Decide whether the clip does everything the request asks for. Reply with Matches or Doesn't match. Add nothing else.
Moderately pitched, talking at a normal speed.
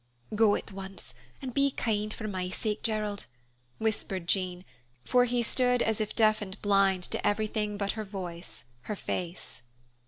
Doesn't match